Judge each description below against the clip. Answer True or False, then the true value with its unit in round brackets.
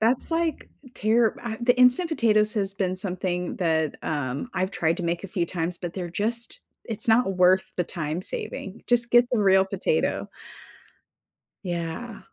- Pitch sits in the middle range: False (195 Hz)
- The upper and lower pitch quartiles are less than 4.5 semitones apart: False (5.1 semitones)